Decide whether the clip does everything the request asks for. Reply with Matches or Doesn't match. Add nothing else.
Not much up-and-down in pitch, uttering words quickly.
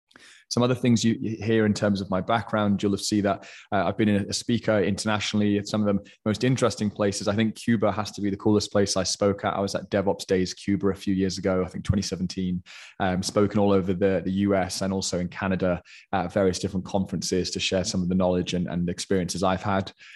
Matches